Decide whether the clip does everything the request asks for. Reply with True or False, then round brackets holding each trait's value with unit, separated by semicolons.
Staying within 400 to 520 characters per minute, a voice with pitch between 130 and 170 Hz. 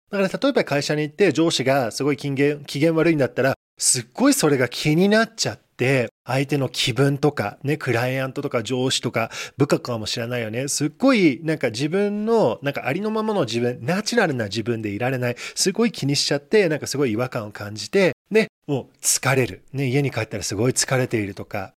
True (420 characters per minute; 140 Hz)